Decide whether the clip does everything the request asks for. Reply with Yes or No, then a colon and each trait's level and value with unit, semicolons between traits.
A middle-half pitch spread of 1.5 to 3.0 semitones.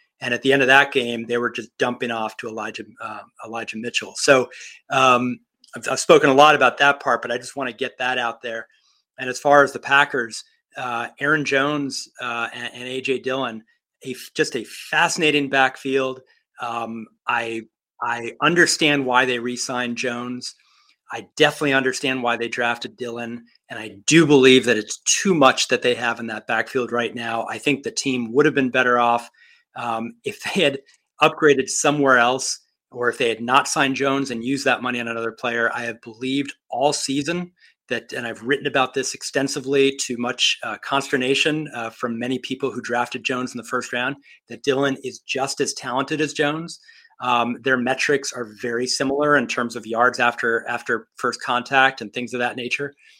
Yes: narrow, 2.6 semitones